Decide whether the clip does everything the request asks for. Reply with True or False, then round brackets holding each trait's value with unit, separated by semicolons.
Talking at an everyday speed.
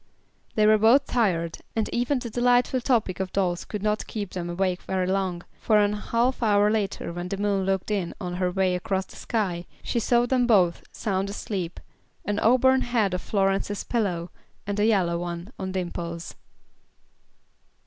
True (175 wpm)